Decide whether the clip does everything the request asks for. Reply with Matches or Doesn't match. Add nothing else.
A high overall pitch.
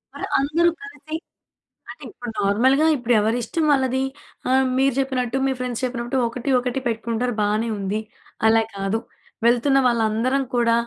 Matches